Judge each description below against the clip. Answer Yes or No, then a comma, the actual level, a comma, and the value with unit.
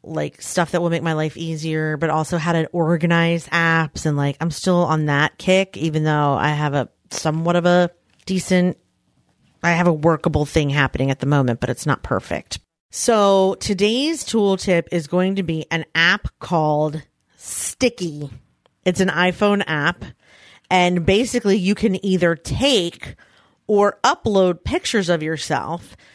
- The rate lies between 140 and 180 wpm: Yes, average, 160 wpm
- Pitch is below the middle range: No, medium, 170 Hz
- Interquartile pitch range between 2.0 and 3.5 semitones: Yes, average, 3.1 semitones